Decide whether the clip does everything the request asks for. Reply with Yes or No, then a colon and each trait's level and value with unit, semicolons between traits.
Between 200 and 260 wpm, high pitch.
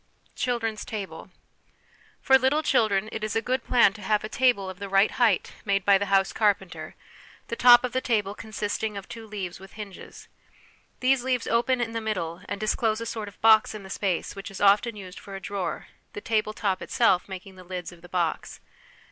Yes: fast, 205 wpm; high, 210 Hz